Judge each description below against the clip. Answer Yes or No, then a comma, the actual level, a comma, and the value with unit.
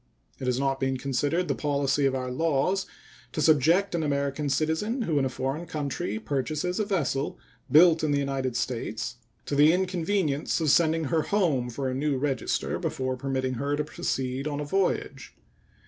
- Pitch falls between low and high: Yes, medium, 145 Hz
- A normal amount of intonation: Yes, average, 3.3 semitones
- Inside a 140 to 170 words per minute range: No, average, 180 wpm